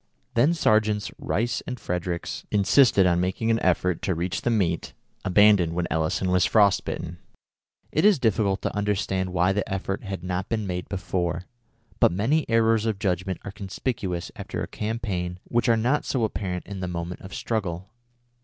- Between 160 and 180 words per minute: Yes, average, 170 wpm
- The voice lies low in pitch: Yes, very low, 95 Hz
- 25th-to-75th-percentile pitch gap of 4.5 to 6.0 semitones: No, average, 3.7 semitones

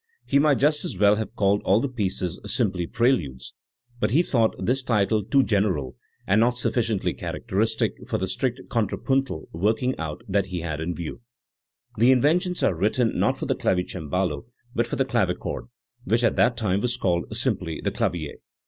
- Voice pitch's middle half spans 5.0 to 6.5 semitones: Yes, average, 5.3 semitones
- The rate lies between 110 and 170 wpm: No, average, 185 wpm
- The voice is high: No, low, 105 Hz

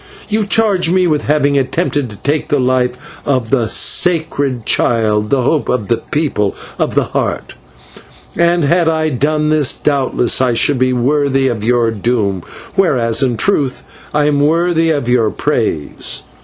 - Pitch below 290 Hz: Yes, medium, 140 Hz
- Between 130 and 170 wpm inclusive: Yes, average, 160 wpm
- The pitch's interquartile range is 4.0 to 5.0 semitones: Yes, average, 4.4 semitones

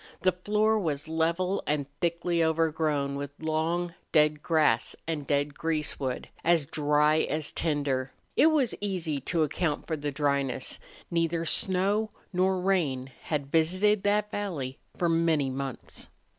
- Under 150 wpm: Yes, slow, 135 wpm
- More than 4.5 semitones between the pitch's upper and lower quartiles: No, average, 3.8 semitones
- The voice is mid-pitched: Yes, medium, 160 Hz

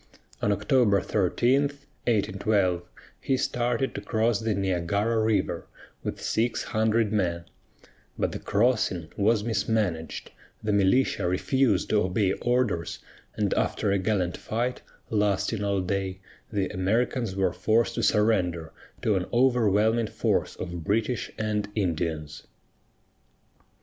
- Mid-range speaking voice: No, low, 105 Hz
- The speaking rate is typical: No, slow, 120 wpm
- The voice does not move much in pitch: No, average, 3.5 semitones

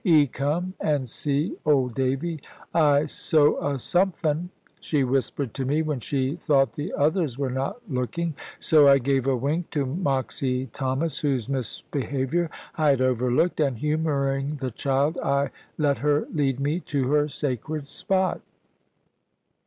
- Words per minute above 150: No, average, 145 wpm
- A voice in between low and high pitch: Yes, medium, 145 Hz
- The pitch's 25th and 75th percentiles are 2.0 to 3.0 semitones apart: Yes, average, 2.7 semitones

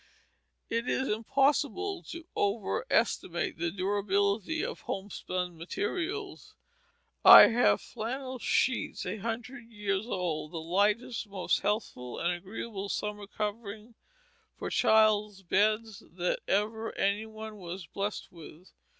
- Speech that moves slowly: Yes, slow, 115 wpm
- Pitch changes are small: No, average, 3.2 semitones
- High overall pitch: Yes, high, 210 Hz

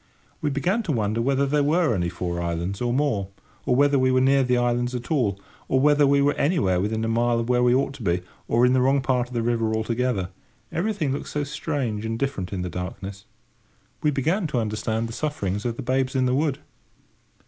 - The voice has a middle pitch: No, low, 125 Hz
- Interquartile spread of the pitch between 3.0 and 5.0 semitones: Yes, average, 4.2 semitones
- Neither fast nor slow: No, fast, 225 wpm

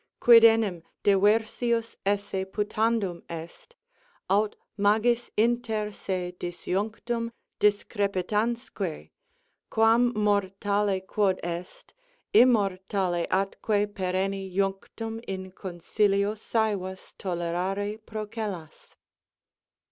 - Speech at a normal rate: No, slow, 75 wpm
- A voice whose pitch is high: Yes, high, 205 Hz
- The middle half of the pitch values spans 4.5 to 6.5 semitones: No, average, 2.8 semitones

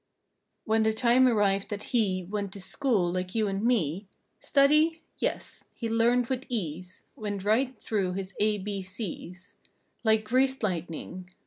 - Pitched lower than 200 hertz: No, high, 210 Hz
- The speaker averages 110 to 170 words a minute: Yes, average, 150 wpm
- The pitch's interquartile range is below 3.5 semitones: No, average, 4.1 semitones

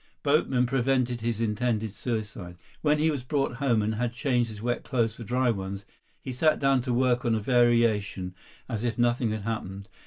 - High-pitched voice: No, low, 120 Hz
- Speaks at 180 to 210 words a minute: Yes, average, 190 wpm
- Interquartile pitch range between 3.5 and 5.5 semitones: No, average, 2.7 semitones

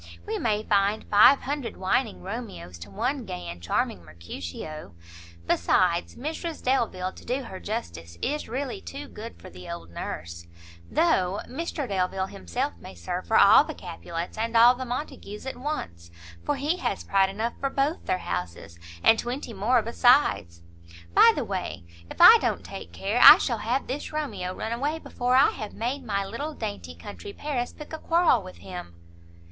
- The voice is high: Yes, high, 220 Hz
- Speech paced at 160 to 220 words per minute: Yes, average, 175 wpm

